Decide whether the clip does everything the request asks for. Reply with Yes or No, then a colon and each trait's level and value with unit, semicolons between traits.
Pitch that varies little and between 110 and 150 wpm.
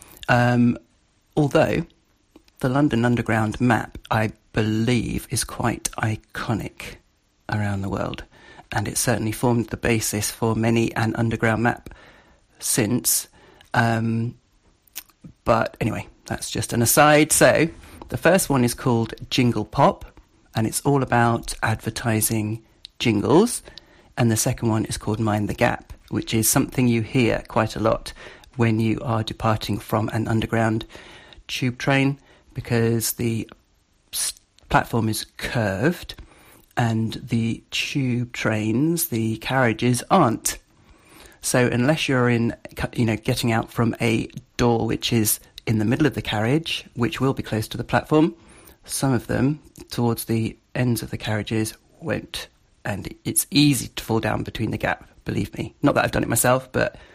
Yes: narrow, 2.1 semitones; average, 145 wpm